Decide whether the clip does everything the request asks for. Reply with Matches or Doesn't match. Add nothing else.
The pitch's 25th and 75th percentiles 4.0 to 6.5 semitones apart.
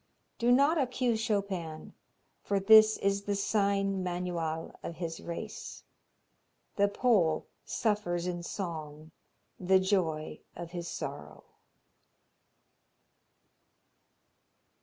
Doesn't match